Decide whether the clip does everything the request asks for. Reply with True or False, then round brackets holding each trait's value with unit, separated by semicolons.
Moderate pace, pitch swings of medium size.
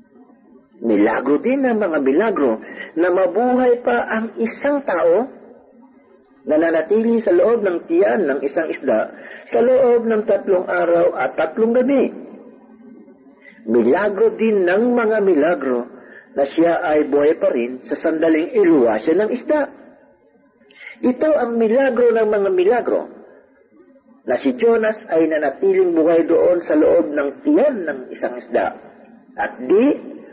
False (130 wpm; 7.0 semitones)